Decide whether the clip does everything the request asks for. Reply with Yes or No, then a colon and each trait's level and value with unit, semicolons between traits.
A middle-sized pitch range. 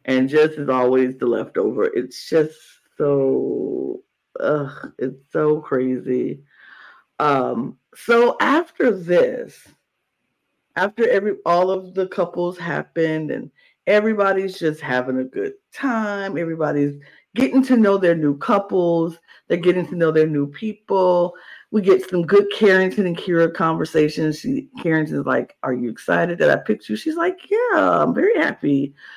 No: wide, 6.0 semitones